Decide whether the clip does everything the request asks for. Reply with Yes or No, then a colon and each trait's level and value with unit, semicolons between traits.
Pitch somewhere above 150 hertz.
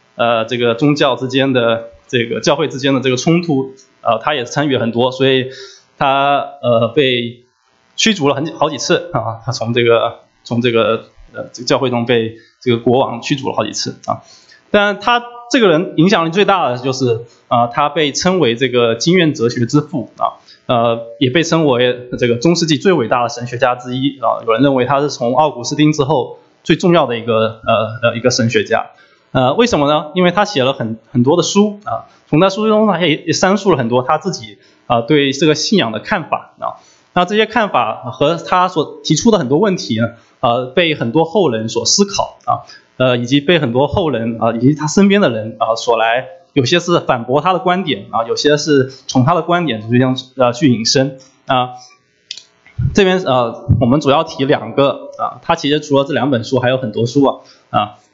No: low, 135 Hz